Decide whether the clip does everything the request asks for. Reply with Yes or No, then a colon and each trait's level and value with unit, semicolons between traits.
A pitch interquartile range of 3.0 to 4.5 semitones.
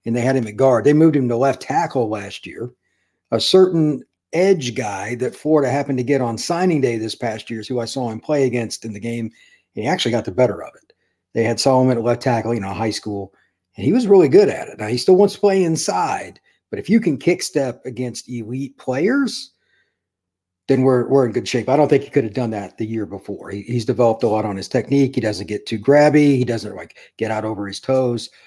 Yes: average, 3.9 semitones